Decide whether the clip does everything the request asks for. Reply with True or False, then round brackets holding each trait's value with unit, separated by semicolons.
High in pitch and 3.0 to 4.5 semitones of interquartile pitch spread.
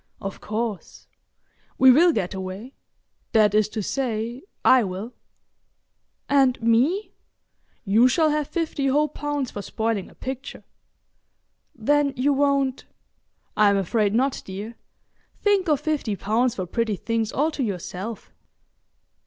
False (235 Hz; 4.9 semitones)